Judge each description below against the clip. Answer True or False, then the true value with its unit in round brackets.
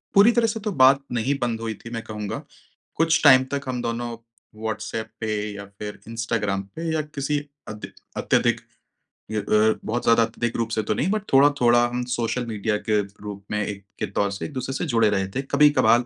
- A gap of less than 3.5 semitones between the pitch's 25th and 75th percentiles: False (3.8 semitones)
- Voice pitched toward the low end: True (115 Hz)